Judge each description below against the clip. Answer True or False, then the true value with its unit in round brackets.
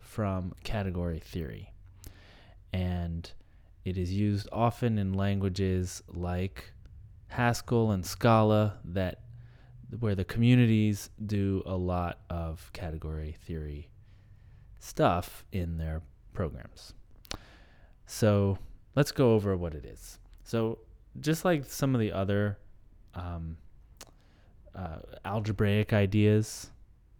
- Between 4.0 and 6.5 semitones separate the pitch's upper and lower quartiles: False (3.1 semitones)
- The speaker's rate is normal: False (100 wpm)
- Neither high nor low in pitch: False (100 Hz)